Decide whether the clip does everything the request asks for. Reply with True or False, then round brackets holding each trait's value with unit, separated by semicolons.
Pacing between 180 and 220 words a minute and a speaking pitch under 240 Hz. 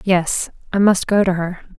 True (200 wpm; 185 Hz)